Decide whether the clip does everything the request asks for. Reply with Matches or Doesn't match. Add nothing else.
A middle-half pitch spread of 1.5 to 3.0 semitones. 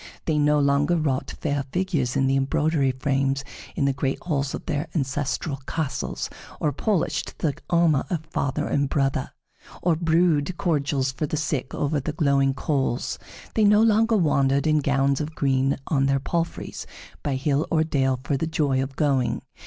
Matches